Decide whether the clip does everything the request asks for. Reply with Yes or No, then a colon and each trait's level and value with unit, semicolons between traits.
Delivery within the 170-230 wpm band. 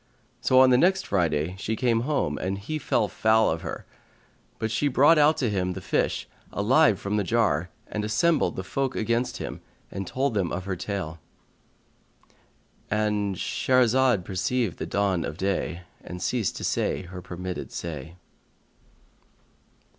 No: average, 150 wpm